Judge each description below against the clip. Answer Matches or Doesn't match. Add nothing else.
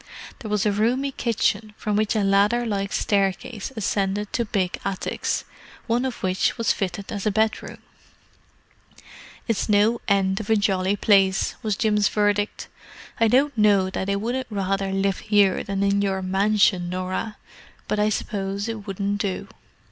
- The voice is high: Matches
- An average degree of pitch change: Doesn't match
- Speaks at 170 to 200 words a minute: Doesn't match